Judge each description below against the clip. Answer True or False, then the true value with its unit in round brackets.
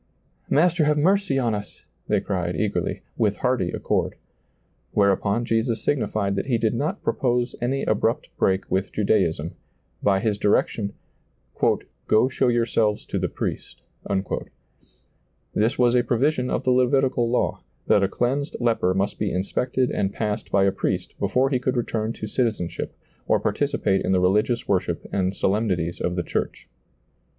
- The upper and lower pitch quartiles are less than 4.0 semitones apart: False (4.3 semitones)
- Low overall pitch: True (110 Hz)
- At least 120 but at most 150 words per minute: False (165 wpm)